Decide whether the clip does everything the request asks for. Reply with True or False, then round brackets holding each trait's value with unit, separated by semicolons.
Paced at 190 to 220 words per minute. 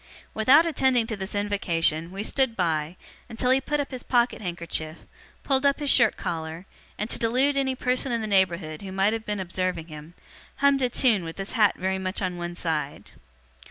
True (195 wpm)